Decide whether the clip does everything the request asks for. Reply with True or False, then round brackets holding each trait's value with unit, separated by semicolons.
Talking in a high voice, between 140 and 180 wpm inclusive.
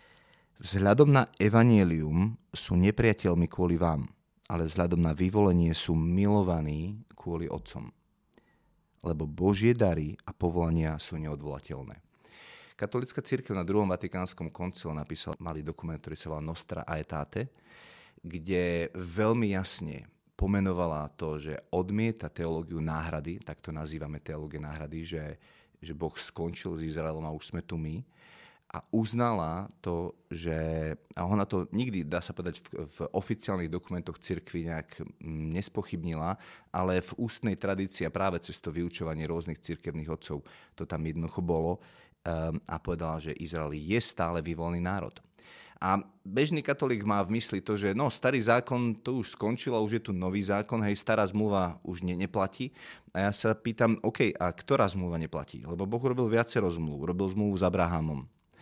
False (90 Hz; 150 wpm)